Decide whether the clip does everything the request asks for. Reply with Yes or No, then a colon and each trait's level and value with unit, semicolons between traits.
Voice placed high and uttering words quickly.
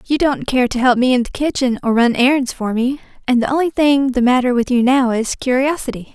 Yes: very high, 255 Hz; fast, 245 wpm